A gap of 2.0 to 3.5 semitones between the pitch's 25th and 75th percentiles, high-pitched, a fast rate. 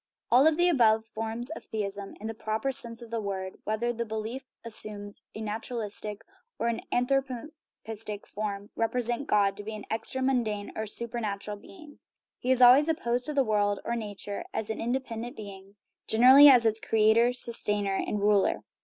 No: average, 2.8 semitones; high, 225 Hz; average, 175 wpm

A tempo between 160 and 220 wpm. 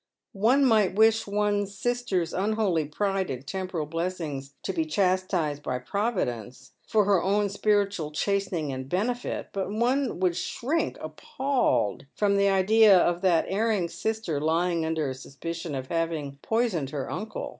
No: average, 145 wpm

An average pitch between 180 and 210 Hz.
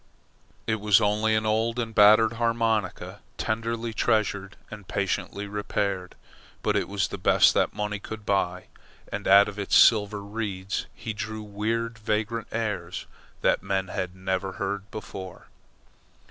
No: low, 105 Hz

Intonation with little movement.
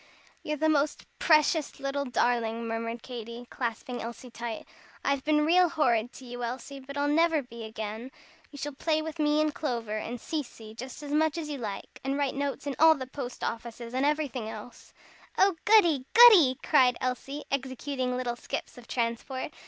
No: average, 4.0 semitones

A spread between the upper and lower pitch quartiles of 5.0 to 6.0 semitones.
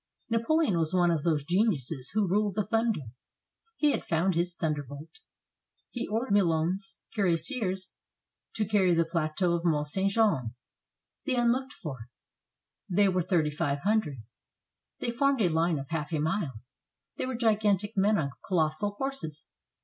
Yes: average, 5.3 semitones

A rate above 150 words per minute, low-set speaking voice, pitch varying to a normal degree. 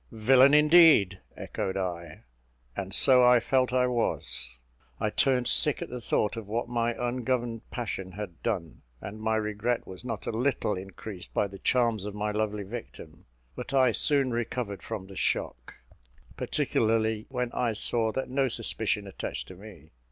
Yes: average, 165 wpm; low, 110 Hz; average, 3.6 semitones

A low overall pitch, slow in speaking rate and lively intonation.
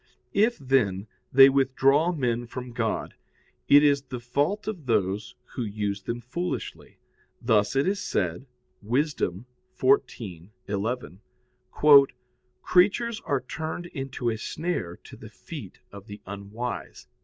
Yes: low, 125 Hz; slow, 120 wpm; wide, 5.7 semitones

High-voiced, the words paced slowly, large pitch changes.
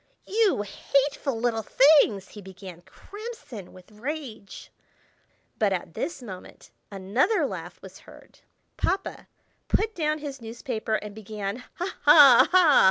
Yes: high, 235 Hz; slow, 125 wpm; wide, 7.1 semitones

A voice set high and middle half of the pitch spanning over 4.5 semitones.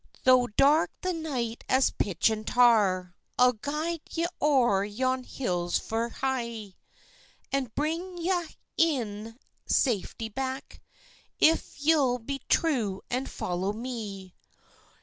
Yes: very high, 250 Hz; average, 4.9 semitones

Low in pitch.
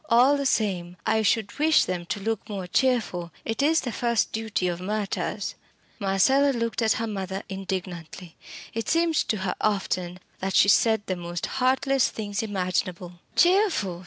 No: high, 205 Hz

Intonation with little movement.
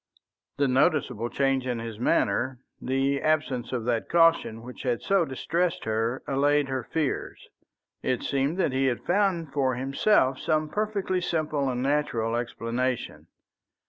No: average, 3.9 semitones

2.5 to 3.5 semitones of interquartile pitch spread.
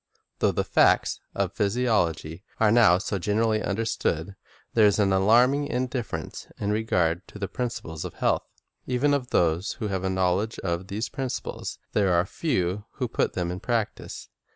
No: average, 4.2 semitones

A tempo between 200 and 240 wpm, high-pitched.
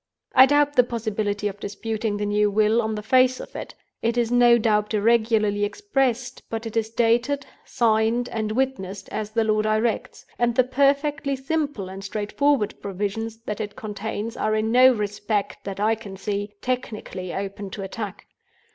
No: average, 170 wpm; high, 220 Hz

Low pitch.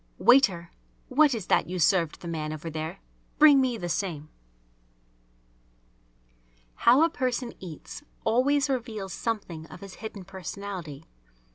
No: high, 195 Hz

